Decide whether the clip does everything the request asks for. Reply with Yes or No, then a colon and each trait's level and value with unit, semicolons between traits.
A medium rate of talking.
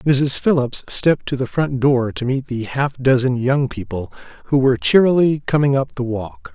Yes: average, 195 wpm